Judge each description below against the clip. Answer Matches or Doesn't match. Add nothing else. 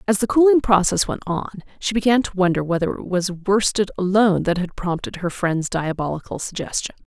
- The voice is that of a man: Doesn't match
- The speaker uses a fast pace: Doesn't match